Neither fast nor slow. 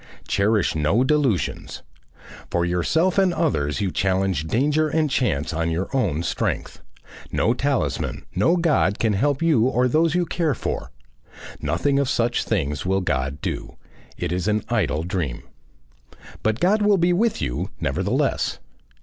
Yes: average, 150 wpm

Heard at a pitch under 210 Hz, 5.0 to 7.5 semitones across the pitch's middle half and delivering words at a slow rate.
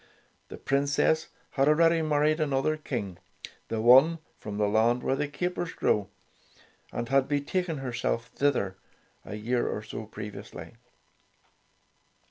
Yes: low, 135 Hz; wide, 5.6 semitones; slow, 130 wpm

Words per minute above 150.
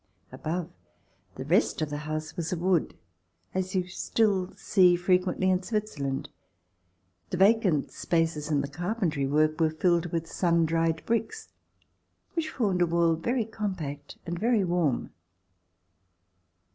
No: average, 140 wpm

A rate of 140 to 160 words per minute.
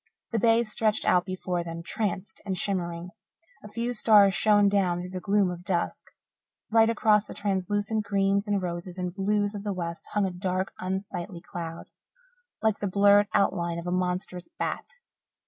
No: average, 170 wpm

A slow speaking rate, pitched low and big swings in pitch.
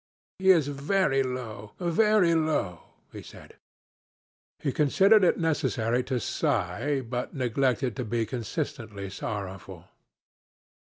Yes: slow, 110 wpm; low, 130 Hz; wide, 6.2 semitones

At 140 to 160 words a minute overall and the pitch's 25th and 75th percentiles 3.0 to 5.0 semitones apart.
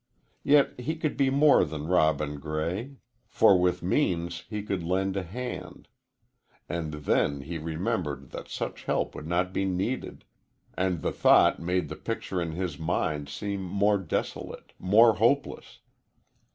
Yes: average, 150 wpm; average, 4.6 semitones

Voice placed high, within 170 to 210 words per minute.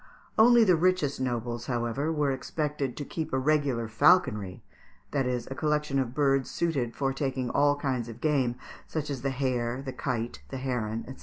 No: low, 135 Hz; average, 180 wpm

